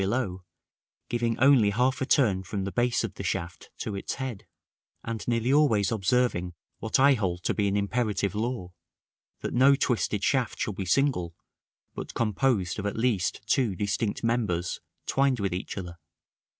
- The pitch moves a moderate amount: Yes, average, 4.5 semitones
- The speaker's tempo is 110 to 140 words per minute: No, average, 165 wpm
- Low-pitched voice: Yes, low, 110 Hz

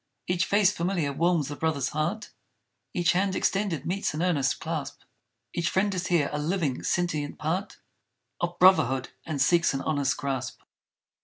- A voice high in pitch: No, medium, 170 Hz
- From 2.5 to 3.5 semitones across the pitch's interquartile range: No, average, 4.0 semitones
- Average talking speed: Yes, average, 155 wpm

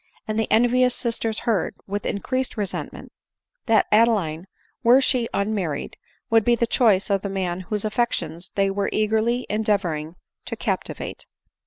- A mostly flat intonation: No, average, 3.2 semitones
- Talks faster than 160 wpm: No, average, 145 wpm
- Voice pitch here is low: No, high, 215 Hz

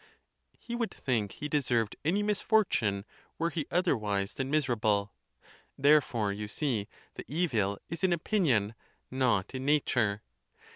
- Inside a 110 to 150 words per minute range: Yes, slow, 135 wpm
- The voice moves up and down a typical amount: No, wide, 7.4 semitones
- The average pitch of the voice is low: Yes, low, 130 Hz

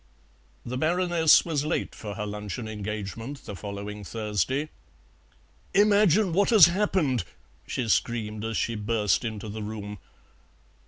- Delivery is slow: Yes, slow, 125 wpm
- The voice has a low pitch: Yes, low, 115 Hz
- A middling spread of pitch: No, wide, 7.1 semitones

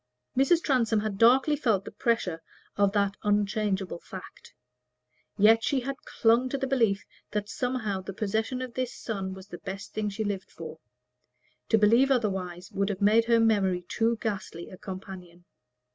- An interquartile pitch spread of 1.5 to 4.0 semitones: Yes, average, 3.2 semitones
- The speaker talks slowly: No, average, 165 wpm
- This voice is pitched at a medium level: No, high, 210 Hz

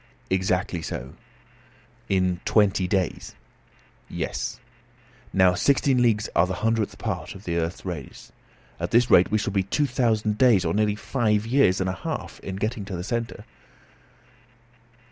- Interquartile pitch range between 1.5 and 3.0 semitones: No, average, 3.4 semitones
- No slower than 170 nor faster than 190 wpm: No, average, 150 wpm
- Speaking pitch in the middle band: No, low, 100 Hz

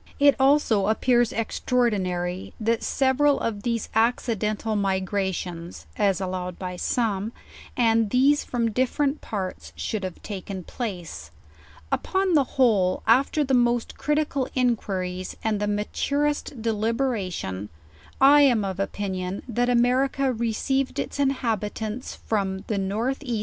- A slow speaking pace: Yes, slow, 130 wpm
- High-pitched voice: Yes, high, 225 Hz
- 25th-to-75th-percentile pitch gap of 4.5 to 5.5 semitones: Yes, average, 4.8 semitones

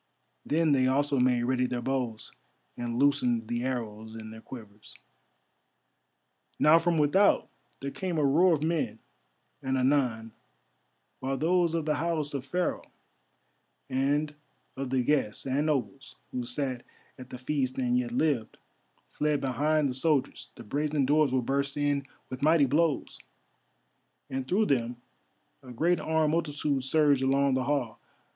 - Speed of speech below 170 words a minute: Yes, average, 150 wpm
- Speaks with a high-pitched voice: No, low, 135 Hz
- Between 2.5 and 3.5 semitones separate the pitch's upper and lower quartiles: Yes, average, 3.2 semitones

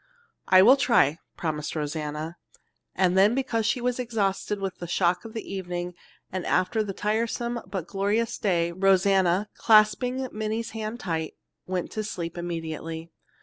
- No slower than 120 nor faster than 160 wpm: Yes, average, 145 wpm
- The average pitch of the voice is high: Yes, high, 195 Hz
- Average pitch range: Yes, average, 4.2 semitones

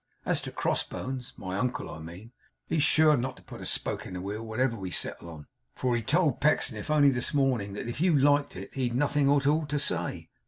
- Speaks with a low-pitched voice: Yes, low, 130 Hz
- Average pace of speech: No, fast, 225 wpm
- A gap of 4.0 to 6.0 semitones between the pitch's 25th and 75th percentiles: Yes, average, 5.3 semitones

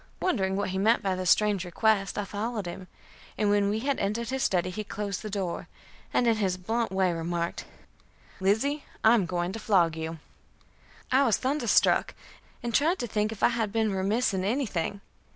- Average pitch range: Yes, average, 3.4 semitones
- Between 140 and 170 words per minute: No, average, 190 wpm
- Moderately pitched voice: No, high, 205 Hz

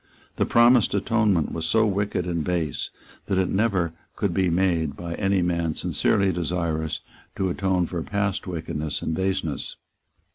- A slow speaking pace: No, average, 150 wpm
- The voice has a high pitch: No, very low, 90 Hz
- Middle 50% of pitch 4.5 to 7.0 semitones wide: No, average, 2.9 semitones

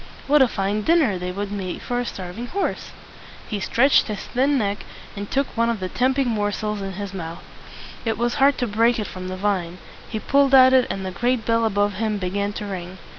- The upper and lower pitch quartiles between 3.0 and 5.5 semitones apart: Yes, average, 4.0 semitones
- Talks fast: Yes, fast, 220 wpm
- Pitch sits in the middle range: No, high, 210 Hz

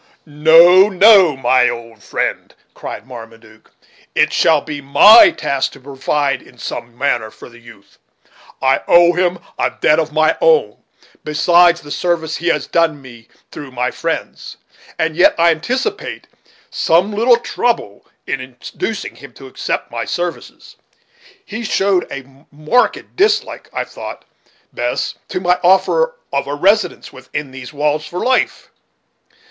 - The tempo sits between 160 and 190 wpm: No, average, 145 wpm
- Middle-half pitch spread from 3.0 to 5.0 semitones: No, wide, 5.5 semitones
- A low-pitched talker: No, medium, 155 Hz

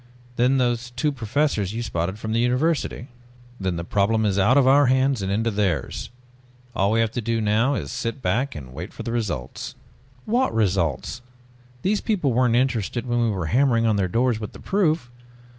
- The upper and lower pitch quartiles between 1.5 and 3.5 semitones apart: No, average, 4.3 semitones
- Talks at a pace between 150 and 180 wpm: No, average, 190 wpm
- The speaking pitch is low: Yes, low, 115 Hz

